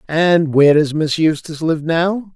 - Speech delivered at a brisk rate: No, average, 180 wpm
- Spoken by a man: Yes, male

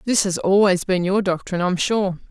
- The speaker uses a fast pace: Yes, fast, 235 wpm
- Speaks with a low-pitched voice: No, high, 190 Hz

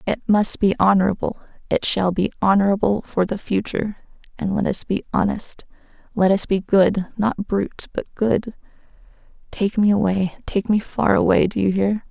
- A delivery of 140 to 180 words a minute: Yes, average, 170 wpm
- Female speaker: Yes, female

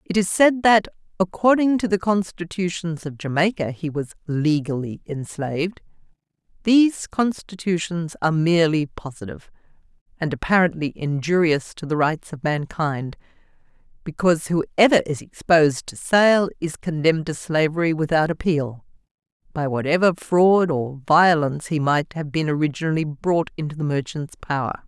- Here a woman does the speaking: Yes, female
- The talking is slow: Yes, slow, 130 wpm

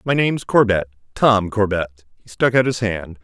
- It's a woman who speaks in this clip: No, male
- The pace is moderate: Yes, average, 165 wpm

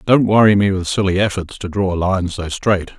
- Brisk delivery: Yes, fast, 240 wpm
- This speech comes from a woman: No, male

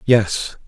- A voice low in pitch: Yes, low, 110 Hz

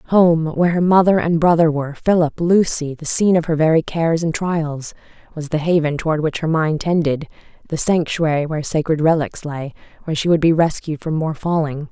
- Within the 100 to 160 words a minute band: No, average, 185 wpm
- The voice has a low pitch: No, medium, 160 Hz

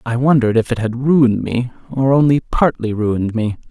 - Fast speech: No, average, 195 wpm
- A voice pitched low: Yes, low, 125 Hz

